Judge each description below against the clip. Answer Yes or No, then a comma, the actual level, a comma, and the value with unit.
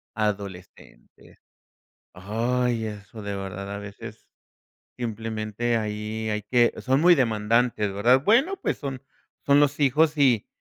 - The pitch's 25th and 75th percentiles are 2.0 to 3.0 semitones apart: No, average, 3.8 semitones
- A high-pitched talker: No, low, 115 Hz